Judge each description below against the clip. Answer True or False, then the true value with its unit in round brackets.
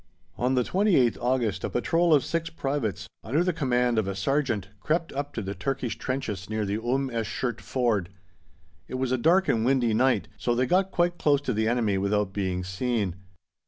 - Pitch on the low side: True (125 Hz)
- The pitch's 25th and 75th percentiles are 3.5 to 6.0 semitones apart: True (4.7 semitones)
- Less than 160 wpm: False (200 wpm)